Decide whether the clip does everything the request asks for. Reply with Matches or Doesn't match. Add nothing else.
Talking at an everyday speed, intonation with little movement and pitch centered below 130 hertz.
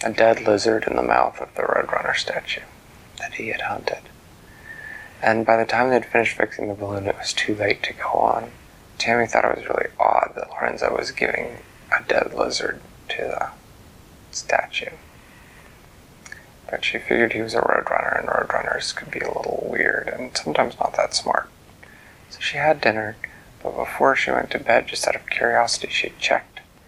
Matches